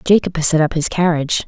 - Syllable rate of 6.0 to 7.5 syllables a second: Yes, 6.8 syllables/s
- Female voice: Yes, female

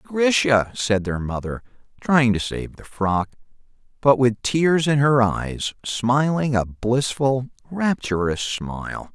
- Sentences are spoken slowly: Yes, slow, 130 wpm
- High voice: No, low, 125 Hz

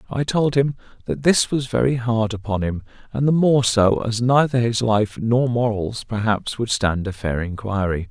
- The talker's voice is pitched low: Yes, low, 115 Hz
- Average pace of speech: Yes, average, 190 wpm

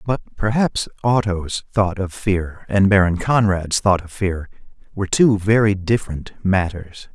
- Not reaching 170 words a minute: Yes, average, 145 wpm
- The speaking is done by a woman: No, male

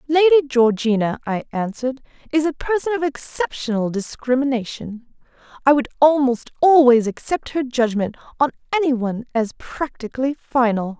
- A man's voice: No, female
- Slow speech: Yes, slow, 120 wpm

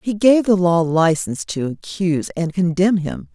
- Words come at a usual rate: Yes, average, 180 wpm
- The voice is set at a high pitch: No, medium, 180 Hz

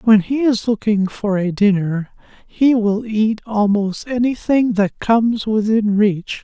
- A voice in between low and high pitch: No, high, 215 Hz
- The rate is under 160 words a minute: Yes, average, 150 wpm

